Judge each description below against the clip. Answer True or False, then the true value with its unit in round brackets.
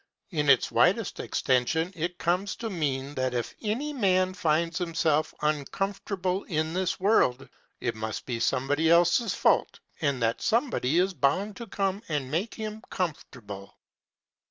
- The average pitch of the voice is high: False (165 Hz)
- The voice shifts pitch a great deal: True (5.9 semitones)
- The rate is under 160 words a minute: True (145 wpm)